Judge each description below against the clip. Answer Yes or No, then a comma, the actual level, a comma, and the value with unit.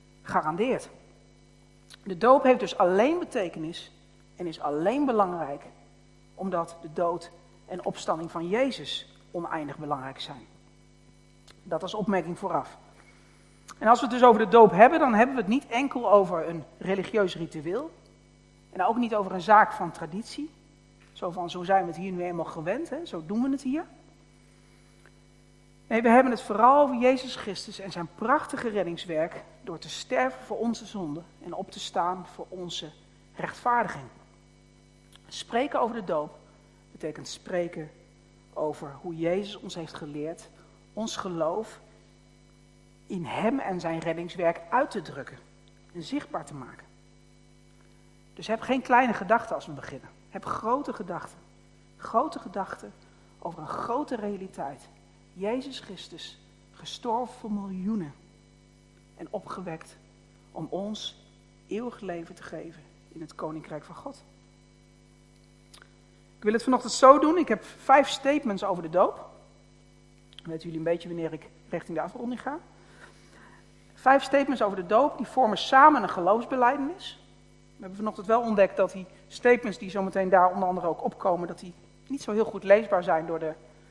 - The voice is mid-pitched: No, high, 195 Hz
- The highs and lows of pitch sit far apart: Yes, wide, 5.9 semitones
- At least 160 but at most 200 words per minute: No, average, 150 wpm